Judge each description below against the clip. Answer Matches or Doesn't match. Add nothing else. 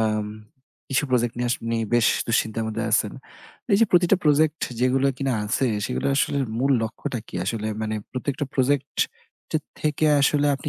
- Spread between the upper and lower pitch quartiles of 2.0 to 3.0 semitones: Doesn't match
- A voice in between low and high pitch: Doesn't match